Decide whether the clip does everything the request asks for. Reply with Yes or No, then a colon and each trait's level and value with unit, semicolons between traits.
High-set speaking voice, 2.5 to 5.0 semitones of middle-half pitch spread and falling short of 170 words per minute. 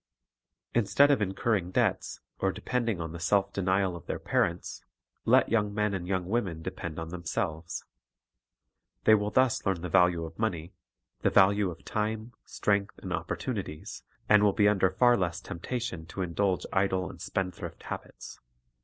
No: very low, 95 Hz; average, 3.3 semitones; average, 160 wpm